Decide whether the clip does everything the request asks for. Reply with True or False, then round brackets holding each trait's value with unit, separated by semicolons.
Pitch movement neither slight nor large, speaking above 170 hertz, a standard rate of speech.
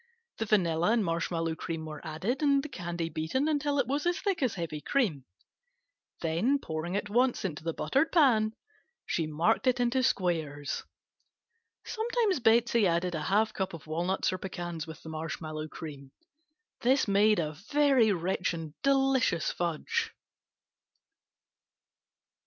False (7.7 semitones; 190 Hz; 145 wpm)